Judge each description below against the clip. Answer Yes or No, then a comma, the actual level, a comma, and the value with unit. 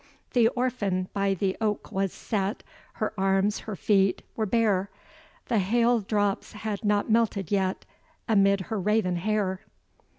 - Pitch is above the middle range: Yes, high, 205 Hz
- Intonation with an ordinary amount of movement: No, narrow, 2.2 semitones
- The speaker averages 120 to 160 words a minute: Yes, average, 140 wpm